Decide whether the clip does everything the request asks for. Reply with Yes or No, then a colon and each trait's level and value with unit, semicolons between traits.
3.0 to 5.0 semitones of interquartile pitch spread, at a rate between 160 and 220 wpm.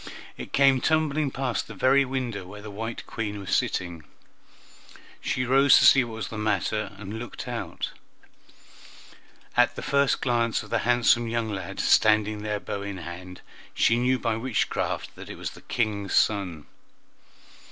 Yes: average, 3.6 semitones; average, 165 wpm